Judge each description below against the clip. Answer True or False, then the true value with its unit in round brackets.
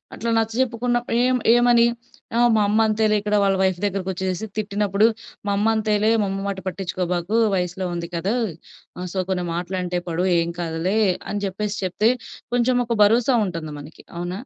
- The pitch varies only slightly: False (3.5 semitones)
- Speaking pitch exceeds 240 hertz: False (200 Hz)